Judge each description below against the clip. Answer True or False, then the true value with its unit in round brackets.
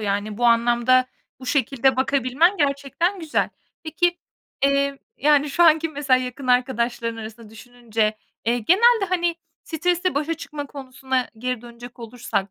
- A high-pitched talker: True (260 Hz)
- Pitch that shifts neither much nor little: True (4.2 semitones)